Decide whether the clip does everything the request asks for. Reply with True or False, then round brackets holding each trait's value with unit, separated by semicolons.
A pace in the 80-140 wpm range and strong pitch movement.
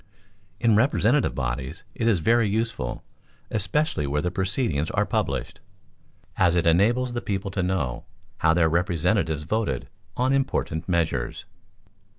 True (135 wpm; 6.1 semitones)